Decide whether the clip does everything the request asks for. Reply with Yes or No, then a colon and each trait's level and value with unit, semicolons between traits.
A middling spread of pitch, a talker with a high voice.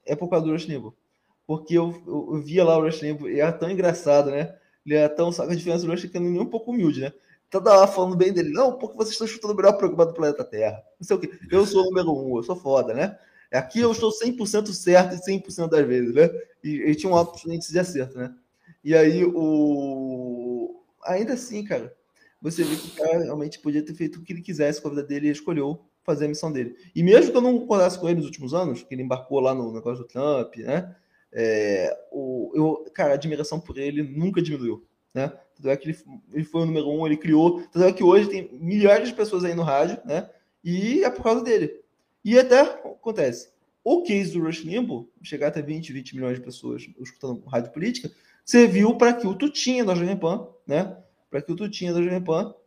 No: average, 4.7 semitones; medium, 165 Hz